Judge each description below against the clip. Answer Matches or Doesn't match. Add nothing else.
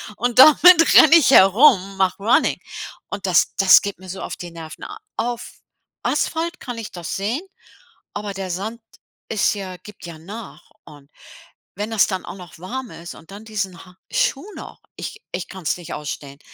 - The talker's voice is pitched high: Matches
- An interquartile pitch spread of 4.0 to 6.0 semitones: Matches